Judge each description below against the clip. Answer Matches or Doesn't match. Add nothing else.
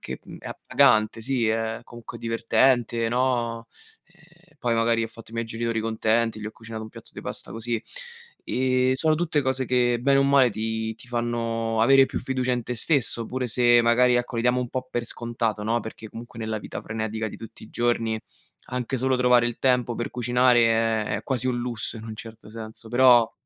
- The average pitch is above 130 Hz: Doesn't match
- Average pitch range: Doesn't match